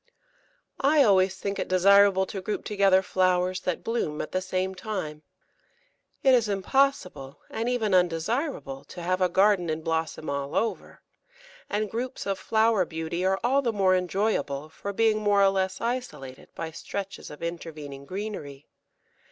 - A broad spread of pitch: No, average, 4.1 semitones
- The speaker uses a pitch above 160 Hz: Yes, high, 190 Hz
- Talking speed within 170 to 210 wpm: No, average, 155 wpm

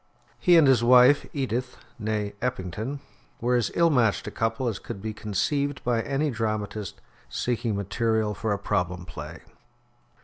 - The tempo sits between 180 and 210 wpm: No, average, 150 wpm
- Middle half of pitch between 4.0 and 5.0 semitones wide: No, average, 3.4 semitones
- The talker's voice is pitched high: No, low, 115 Hz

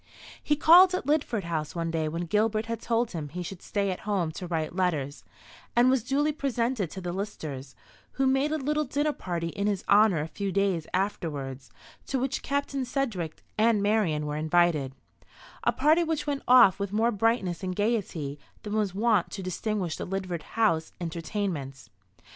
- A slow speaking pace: No, average, 180 wpm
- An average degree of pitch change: No, wide, 6.2 semitones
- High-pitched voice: Yes, high, 200 Hz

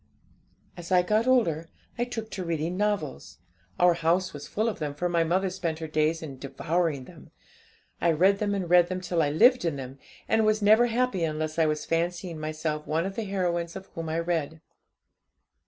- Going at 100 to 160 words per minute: No, average, 200 wpm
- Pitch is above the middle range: No, medium, 170 Hz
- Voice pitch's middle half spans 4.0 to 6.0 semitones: No, average, 3.6 semitones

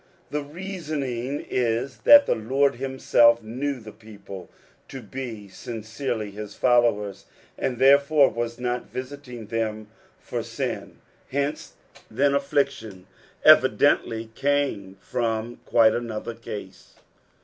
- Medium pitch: No, low, 120 Hz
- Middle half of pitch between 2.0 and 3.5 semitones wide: No, average, 3.9 semitones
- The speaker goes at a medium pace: No, slow, 110 wpm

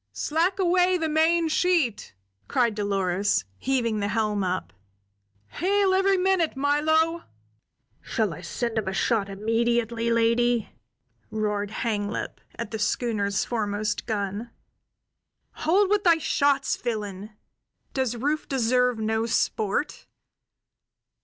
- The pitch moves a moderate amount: No, wide, 6.9 semitones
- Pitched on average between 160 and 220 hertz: No, high, 235 Hz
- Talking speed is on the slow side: Yes, slow, 115 wpm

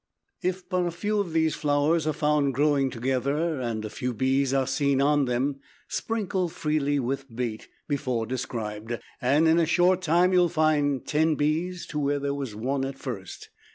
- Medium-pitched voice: Yes, medium, 145 Hz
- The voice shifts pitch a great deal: No, average, 3.7 semitones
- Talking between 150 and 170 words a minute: No, average, 185 wpm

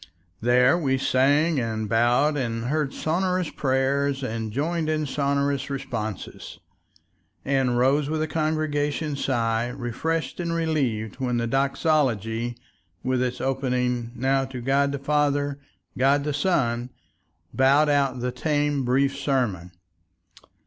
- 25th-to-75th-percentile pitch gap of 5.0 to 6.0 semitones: No, average, 3.0 semitones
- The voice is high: No, low, 135 Hz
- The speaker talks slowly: Yes, slow, 125 wpm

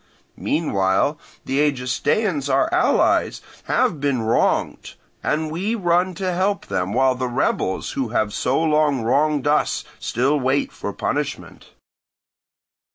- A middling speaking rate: No, slow, 125 wpm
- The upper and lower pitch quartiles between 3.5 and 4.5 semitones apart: Yes, average, 4.2 semitones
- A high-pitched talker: No, medium, 145 Hz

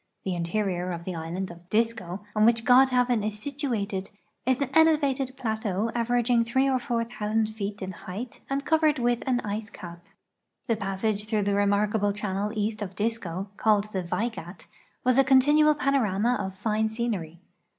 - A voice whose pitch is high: Yes, high, 215 Hz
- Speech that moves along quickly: No, average, 165 wpm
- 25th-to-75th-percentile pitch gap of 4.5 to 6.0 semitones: No, average, 3.8 semitones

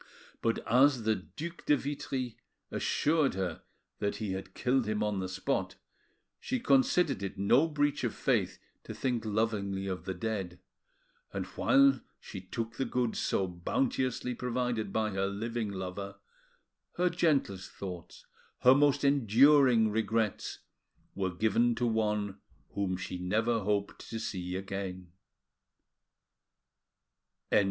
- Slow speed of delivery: Yes, slow, 130 wpm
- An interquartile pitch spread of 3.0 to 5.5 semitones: Yes, average, 4.9 semitones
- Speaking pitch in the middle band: No, low, 110 Hz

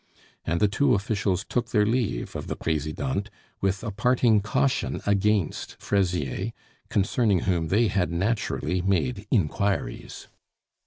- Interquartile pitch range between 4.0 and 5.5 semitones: No, average, 3.4 semitones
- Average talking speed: No, slow, 125 wpm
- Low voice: Yes, low, 100 Hz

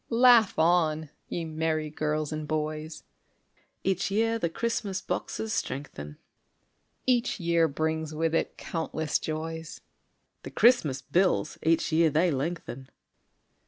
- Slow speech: Yes, slow, 125 wpm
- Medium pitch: Yes, medium, 160 Hz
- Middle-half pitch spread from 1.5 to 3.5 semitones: Yes, average, 2.8 semitones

